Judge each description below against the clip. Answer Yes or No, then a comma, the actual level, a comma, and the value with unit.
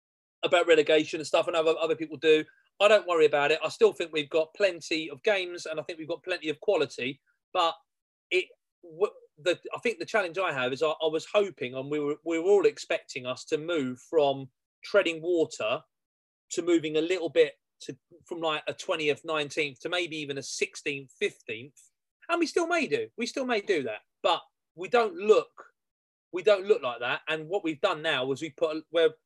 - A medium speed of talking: No, fast, 215 wpm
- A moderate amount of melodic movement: No, wide, 5.7 semitones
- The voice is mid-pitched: Yes, medium, 165 Hz